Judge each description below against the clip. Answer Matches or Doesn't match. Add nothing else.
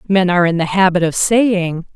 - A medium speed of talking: Doesn't match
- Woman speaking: Matches